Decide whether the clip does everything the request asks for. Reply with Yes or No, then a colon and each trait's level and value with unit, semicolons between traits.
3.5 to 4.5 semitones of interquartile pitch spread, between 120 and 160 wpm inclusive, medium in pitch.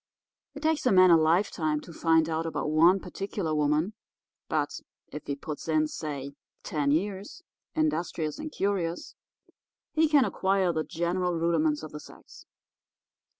Yes: average, 3.9 semitones; average, 150 wpm; medium, 165 Hz